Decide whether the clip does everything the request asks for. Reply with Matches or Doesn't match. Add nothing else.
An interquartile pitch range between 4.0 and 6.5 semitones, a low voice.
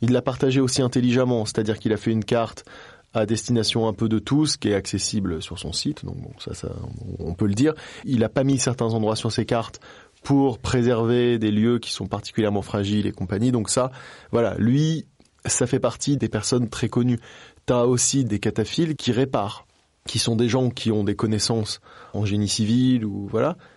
Doesn't match